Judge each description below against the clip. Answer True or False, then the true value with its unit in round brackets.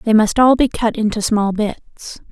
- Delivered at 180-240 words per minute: True (205 wpm)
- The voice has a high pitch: True (220 Hz)